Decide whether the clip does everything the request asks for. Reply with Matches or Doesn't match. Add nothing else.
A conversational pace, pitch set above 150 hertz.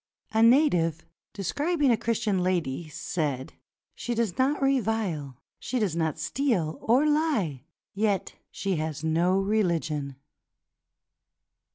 Doesn't match